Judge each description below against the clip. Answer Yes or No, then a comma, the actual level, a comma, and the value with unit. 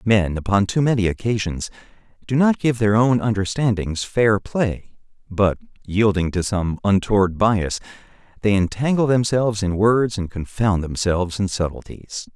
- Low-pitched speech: Yes, low, 105 Hz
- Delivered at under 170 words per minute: Yes, average, 140 wpm